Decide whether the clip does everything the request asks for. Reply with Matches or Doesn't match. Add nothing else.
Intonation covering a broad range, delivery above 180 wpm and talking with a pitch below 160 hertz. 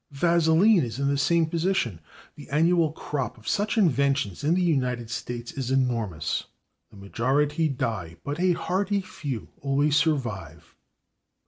Doesn't match